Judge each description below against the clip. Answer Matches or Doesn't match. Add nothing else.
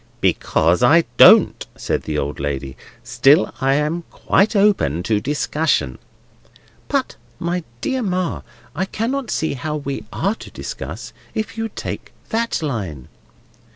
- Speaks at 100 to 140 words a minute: Matches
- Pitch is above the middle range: Doesn't match